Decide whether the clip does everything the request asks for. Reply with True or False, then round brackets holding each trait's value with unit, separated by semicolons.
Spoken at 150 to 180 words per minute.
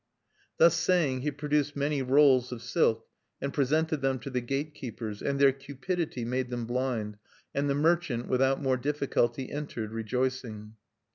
True (155 wpm)